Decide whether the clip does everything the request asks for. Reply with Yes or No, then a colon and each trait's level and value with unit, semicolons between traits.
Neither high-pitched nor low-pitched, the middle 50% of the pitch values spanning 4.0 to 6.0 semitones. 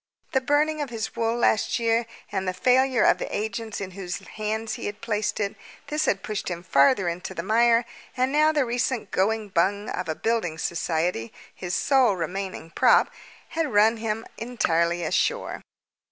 No: high, 215 Hz; average, 4.4 semitones